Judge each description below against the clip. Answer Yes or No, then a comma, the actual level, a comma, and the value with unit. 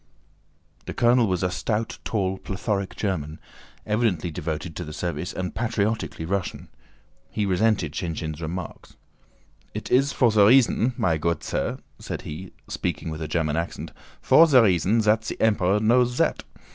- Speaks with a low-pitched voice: Yes, very low, 95 Hz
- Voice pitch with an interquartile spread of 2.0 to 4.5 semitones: No, average, 4.9 semitones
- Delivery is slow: No, average, 155 wpm